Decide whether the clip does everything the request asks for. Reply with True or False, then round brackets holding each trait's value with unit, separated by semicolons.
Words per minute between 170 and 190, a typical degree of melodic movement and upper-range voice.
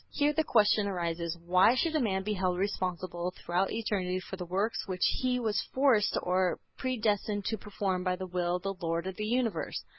False (200 wpm; 3.3 semitones; 195 Hz)